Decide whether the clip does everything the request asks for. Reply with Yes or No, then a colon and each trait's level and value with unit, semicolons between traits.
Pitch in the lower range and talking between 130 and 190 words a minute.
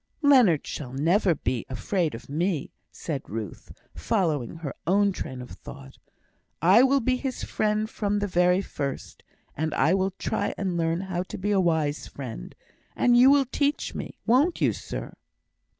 No: medium, 180 Hz; average, 165 wpm